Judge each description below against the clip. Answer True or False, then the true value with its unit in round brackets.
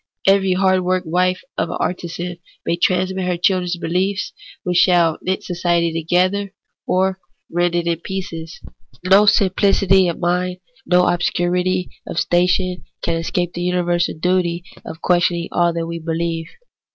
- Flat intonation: True (1.4 semitones)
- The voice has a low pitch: False (180 Hz)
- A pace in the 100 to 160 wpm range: True (150 wpm)